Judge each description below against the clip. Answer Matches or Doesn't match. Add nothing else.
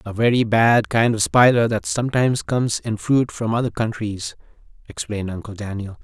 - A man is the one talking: Matches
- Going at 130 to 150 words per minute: Doesn't match